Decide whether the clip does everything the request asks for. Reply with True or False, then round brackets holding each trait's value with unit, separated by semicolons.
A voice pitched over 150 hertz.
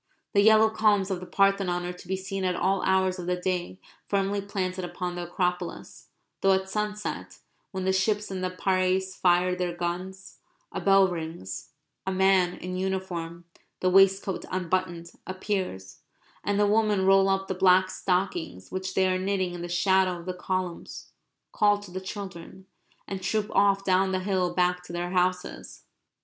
True (185 Hz)